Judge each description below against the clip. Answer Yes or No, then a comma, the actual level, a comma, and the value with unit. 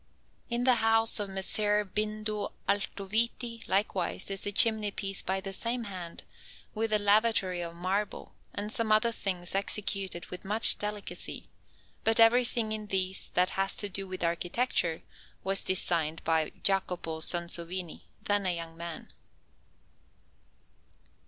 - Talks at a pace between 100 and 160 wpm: Yes, slow, 135 wpm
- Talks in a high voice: Yes, high, 195 Hz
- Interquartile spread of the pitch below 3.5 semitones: Yes, average, 2.9 semitones